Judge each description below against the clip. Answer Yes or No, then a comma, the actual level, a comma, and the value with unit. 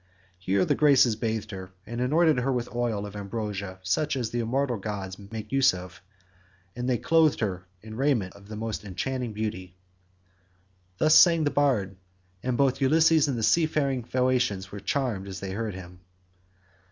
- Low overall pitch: Yes, low, 115 Hz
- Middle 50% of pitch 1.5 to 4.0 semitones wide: No, average, 5.1 semitones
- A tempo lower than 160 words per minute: No, average, 170 wpm